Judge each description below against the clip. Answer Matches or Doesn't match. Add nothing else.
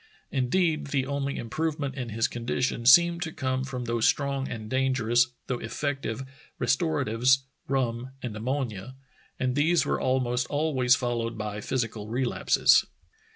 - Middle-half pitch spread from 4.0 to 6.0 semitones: Doesn't match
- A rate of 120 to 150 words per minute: Matches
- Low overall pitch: Matches